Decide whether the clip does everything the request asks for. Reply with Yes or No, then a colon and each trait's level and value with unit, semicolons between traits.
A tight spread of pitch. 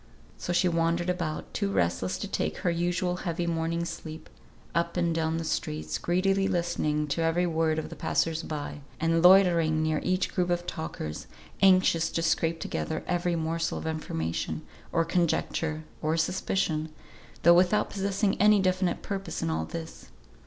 Yes: narrow, 2.1 semitones